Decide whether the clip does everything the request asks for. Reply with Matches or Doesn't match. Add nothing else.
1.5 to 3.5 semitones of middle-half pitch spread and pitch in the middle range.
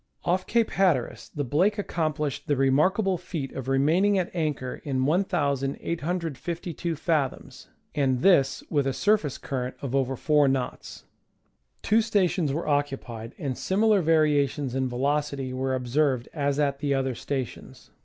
Doesn't match